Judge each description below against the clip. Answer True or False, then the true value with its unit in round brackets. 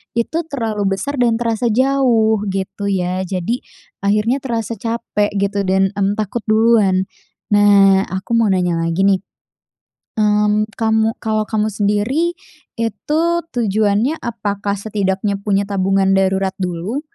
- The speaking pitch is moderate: False (210 Hz)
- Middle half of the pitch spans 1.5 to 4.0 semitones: True (2.8 semitones)